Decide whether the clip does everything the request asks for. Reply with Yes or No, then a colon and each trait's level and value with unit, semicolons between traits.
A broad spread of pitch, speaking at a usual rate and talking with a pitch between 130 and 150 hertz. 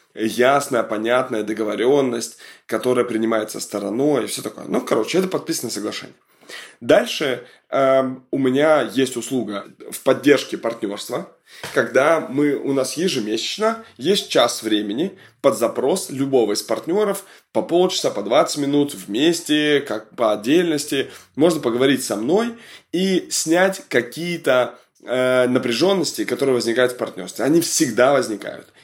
Yes: wide, 5.9 semitones; average, 125 wpm; low, 135 Hz